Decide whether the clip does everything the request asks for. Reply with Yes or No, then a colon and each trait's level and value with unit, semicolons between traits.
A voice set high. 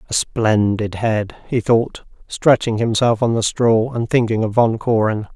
No: low, 115 Hz